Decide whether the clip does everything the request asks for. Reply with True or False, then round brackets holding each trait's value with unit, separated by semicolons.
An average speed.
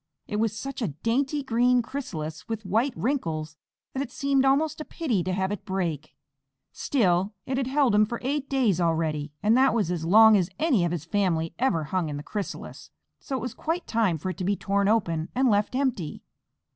False (210 wpm)